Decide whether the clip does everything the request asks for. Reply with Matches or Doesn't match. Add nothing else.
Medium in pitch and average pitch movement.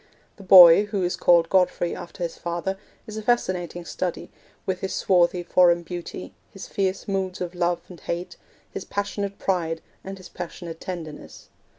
Doesn't match